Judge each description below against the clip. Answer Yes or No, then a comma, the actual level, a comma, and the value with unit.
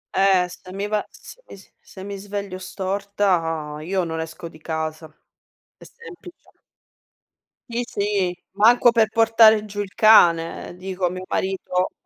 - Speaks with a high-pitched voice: Yes, high, 195 Hz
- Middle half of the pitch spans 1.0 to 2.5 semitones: No, average, 2.9 semitones